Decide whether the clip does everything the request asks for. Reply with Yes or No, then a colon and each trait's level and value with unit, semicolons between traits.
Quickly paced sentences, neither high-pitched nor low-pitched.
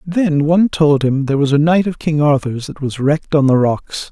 Yes: fast, 250 wpm; medium, 150 Hz